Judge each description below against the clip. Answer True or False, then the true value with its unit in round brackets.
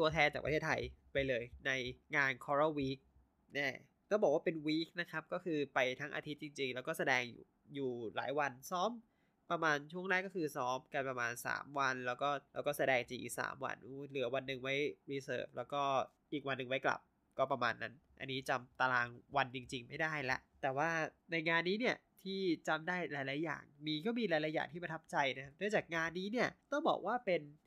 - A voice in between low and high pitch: True (145 Hz)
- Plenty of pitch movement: False (3.9 semitones)